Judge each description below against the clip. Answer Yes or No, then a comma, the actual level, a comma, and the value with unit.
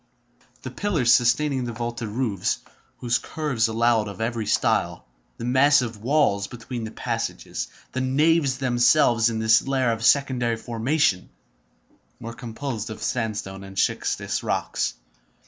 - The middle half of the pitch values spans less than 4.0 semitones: Yes, average, 2.9 semitones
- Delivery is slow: Yes, slow, 130 wpm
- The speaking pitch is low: Yes, low, 120 Hz